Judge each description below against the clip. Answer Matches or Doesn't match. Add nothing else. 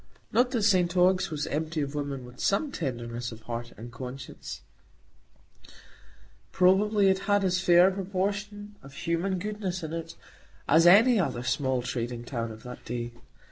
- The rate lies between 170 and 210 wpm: Doesn't match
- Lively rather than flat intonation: Matches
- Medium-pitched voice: Matches